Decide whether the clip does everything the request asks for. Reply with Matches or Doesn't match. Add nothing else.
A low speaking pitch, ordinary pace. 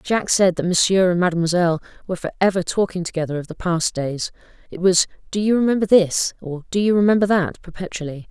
Doesn't match